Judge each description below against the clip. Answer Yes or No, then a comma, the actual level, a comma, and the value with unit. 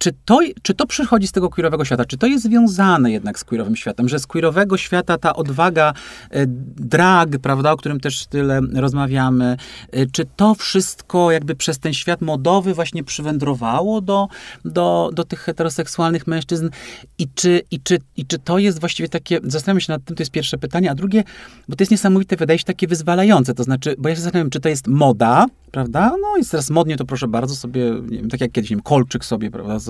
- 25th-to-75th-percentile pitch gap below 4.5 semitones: No, average, 5.2 semitones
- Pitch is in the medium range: Yes, medium, 160 Hz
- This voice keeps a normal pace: No, fast, 210 wpm